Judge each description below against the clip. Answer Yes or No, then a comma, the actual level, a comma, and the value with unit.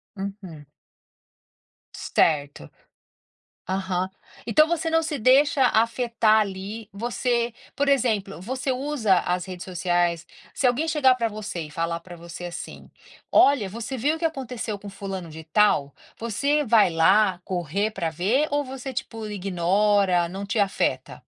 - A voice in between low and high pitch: No, high, 210 Hz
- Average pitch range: No, wide, 5.8 semitones